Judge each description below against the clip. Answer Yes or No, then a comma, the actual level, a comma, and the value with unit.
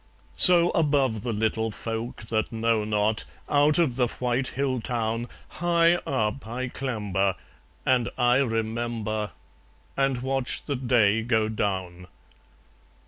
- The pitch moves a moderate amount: Yes, average, 3.3 semitones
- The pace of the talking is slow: Yes, slow, 125 wpm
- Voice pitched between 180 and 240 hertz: No, low, 120 Hz